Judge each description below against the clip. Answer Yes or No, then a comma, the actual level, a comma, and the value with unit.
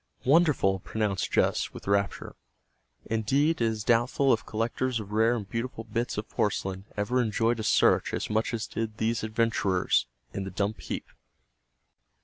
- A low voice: Yes, low, 110 Hz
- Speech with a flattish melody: Yes, narrow, 2.3 semitones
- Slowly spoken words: No, average, 155 wpm